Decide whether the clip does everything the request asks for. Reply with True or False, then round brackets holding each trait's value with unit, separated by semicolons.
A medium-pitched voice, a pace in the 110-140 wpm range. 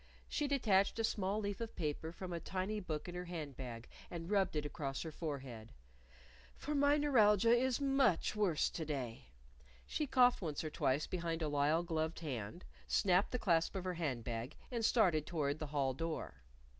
False (170 Hz; 185 wpm)